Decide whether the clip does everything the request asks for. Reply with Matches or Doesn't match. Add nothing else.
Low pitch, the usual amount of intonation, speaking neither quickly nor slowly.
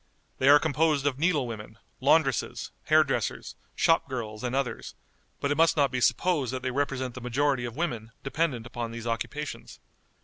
Matches